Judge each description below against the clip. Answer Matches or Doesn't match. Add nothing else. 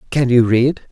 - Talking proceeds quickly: Doesn't match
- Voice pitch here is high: Doesn't match